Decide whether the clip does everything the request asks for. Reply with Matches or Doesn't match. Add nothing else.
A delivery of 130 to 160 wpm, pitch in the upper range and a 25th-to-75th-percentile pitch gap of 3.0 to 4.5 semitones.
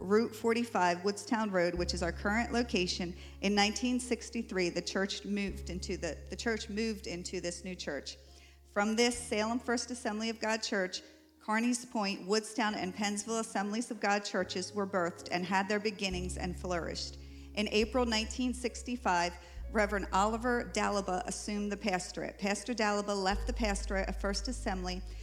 Matches